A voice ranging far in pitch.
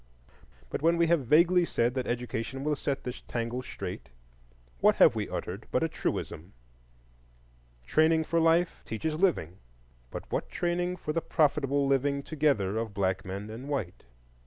Yes: wide, 6.0 semitones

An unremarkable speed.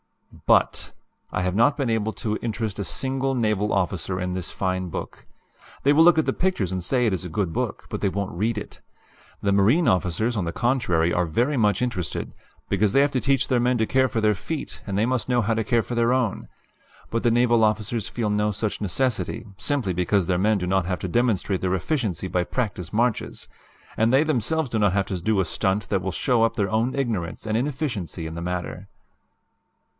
No: fast, 225 wpm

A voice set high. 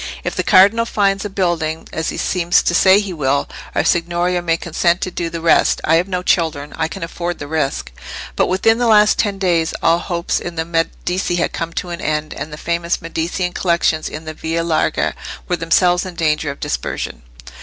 No: medium, 170 Hz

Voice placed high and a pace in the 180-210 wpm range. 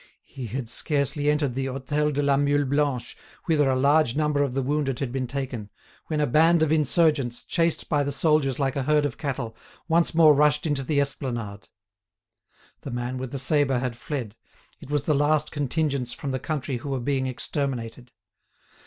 No: medium, 140 Hz; average, 190 wpm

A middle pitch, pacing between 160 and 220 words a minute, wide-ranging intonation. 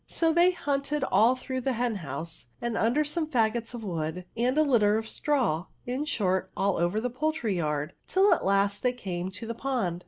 No: high, 230 Hz; average, 195 wpm; wide, 6.4 semitones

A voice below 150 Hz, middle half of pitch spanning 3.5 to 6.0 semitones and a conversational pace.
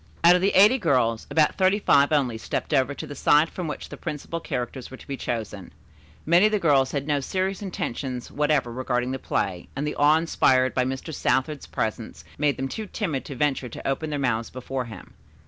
No: medium, 140 Hz; average, 3.9 semitones; fast, 215 wpm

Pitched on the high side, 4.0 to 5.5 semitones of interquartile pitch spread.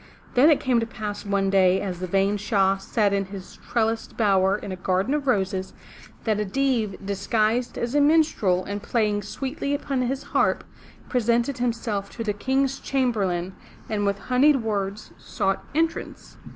Yes: high, 215 Hz; average, 4.3 semitones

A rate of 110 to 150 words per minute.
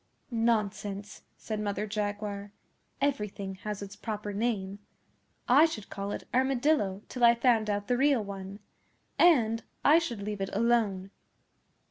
Yes: slow, 135 wpm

